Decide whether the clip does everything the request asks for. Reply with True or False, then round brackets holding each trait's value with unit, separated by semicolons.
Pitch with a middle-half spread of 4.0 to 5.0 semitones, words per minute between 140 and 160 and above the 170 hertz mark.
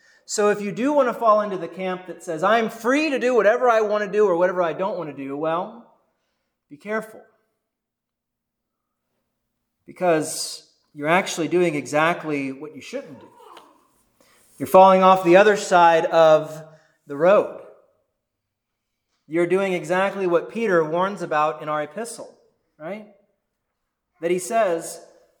True (4.5 semitones; 150 wpm; 185 Hz)